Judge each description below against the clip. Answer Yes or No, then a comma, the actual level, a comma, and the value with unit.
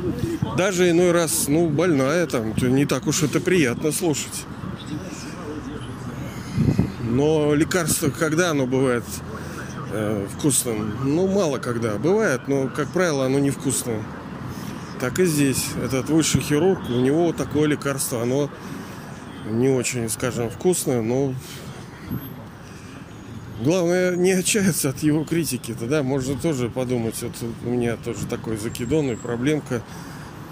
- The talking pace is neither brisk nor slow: Yes, average, 125 wpm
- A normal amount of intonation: Yes, average, 4.8 semitones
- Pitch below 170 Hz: Yes, low, 135 Hz